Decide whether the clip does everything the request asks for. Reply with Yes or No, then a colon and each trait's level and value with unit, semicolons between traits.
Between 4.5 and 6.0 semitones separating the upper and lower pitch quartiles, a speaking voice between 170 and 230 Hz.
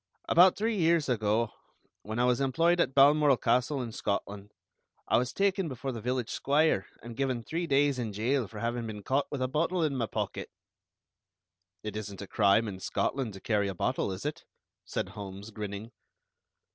No: average, 5.3 semitones; low, 125 Hz